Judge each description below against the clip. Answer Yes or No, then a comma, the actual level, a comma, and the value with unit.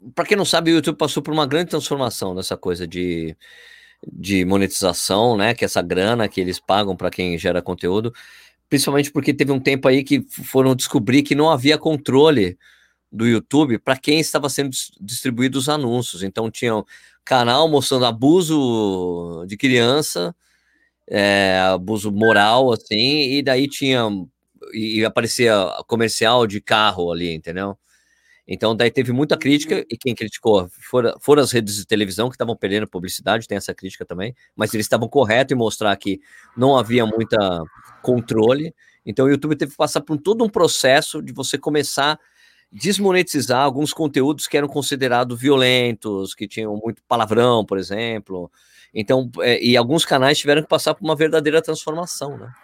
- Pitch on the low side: Yes, low, 125 Hz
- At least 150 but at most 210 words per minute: Yes, average, 165 wpm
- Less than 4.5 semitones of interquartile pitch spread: No, wide, 5.6 semitones